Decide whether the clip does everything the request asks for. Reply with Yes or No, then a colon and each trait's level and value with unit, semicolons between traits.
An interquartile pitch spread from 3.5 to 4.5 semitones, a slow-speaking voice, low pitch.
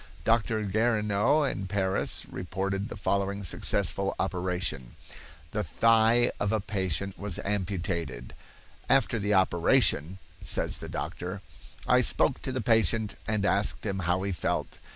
No: narrow, 2.6 semitones; slow, 130 wpm; low, 100 Hz